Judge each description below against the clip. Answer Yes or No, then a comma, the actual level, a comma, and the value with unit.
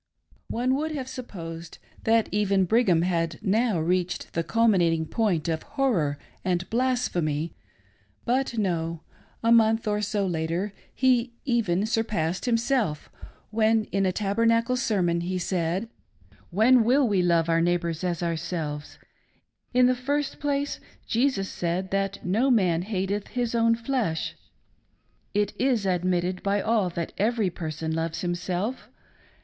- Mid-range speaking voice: No, high, 195 Hz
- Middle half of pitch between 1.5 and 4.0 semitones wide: No, average, 5.2 semitones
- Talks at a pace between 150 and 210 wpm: No, average, 140 wpm